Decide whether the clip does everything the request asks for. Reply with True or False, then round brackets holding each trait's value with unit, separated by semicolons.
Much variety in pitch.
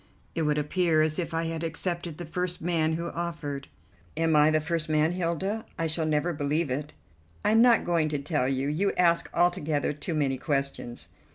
False (2.4 semitones)